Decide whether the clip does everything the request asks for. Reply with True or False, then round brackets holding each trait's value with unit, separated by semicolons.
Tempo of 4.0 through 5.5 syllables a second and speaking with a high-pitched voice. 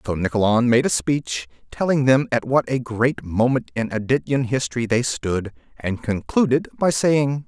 False (4.7 syllables/s; 120 Hz)